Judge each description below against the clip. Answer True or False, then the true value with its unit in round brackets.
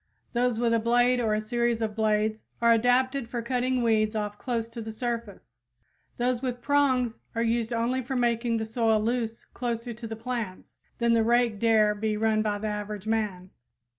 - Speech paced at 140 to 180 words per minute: False (190 wpm)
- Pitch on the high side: True (230 Hz)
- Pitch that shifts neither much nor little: False (1.9 semitones)